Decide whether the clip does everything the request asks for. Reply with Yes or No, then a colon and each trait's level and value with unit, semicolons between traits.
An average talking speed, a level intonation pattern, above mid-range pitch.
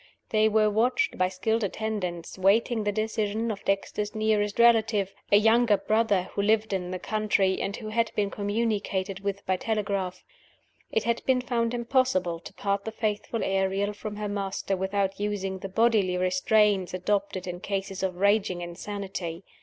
Yes: average, 160 wpm; narrow, 2.3 semitones; high, 205 Hz